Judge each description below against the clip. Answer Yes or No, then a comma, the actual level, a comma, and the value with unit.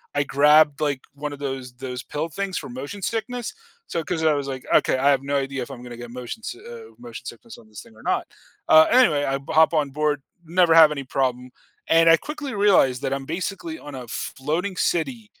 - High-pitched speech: No, medium, 150 Hz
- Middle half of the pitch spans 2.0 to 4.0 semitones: No, average, 5.3 semitones